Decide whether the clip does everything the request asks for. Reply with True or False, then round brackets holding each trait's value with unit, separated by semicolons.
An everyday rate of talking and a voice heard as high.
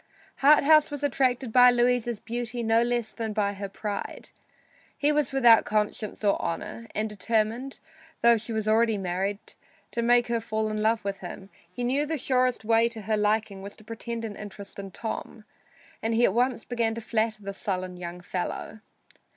True (185 wpm; 225 Hz)